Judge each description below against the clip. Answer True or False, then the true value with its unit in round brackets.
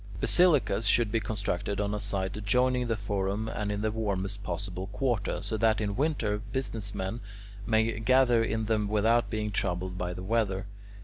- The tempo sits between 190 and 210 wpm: False (175 wpm)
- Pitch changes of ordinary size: False (2.2 semitones)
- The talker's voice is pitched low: True (105 Hz)